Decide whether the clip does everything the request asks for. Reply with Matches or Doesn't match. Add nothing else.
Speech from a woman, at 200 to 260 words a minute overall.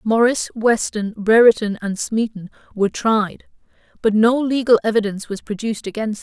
Doesn't match